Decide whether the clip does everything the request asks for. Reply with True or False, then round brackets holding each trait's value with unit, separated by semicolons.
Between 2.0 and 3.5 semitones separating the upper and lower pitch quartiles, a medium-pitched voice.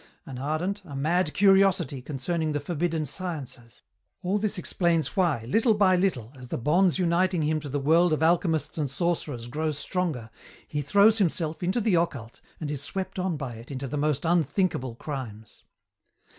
False (4.7 semitones; 160 Hz)